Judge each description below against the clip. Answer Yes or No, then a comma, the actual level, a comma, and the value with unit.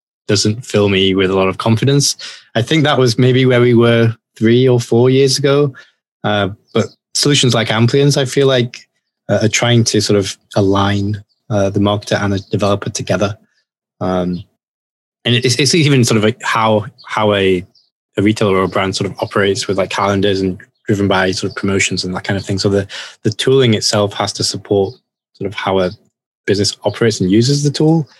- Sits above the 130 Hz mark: No, low, 105 Hz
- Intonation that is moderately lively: Yes, average, 3.8 semitones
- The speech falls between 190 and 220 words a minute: Yes, average, 200 wpm